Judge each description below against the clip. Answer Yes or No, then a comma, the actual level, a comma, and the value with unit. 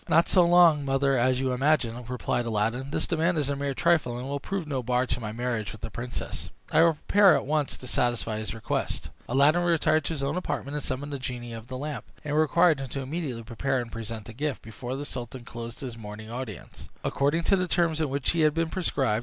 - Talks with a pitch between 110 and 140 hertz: Yes, low, 135 Hz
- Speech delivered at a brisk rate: Yes, fast, 235 wpm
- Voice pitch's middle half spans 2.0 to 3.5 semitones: No, average, 4.4 semitones